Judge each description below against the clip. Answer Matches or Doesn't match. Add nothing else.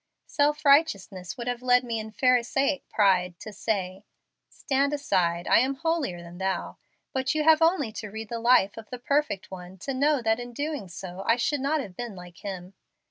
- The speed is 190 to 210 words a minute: Matches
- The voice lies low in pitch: Doesn't match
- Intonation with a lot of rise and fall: Matches